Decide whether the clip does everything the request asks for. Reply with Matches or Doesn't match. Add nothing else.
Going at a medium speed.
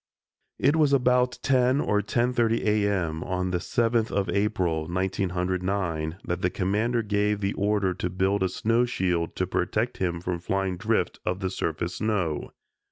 Matches